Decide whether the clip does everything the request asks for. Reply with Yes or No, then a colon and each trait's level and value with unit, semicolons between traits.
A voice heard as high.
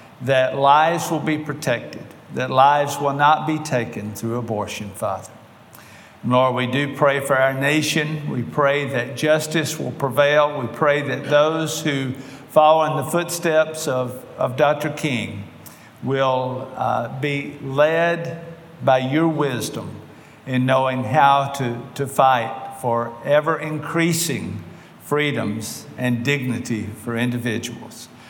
No: medium, 140 Hz